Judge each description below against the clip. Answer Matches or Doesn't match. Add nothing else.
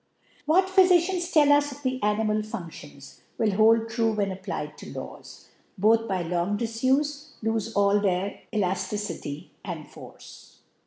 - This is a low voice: Doesn't match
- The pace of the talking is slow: Matches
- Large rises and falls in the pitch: Matches